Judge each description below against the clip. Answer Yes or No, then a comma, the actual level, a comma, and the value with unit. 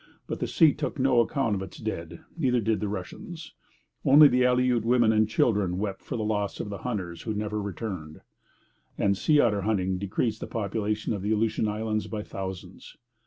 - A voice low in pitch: Yes, low, 110 Hz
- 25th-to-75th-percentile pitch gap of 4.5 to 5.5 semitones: No, average, 3.1 semitones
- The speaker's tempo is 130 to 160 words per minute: No, average, 190 wpm